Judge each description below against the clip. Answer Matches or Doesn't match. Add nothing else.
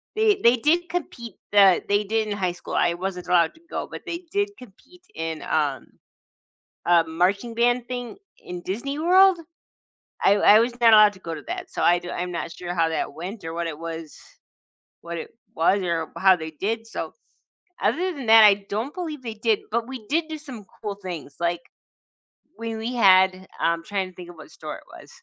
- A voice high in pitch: Matches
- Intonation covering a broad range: Matches